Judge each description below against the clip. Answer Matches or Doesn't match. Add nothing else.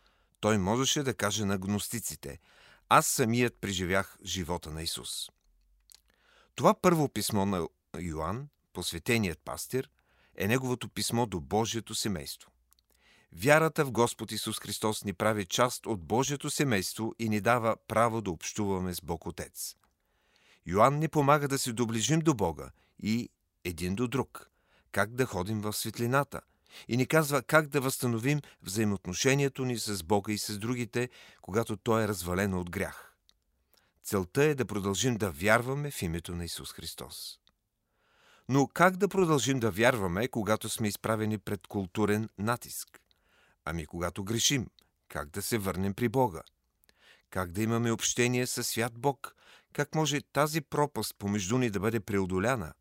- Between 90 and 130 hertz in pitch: Matches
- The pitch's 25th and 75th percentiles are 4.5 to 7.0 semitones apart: Matches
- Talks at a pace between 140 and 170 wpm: Matches